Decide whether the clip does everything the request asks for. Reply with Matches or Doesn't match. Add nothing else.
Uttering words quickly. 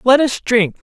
Doesn't match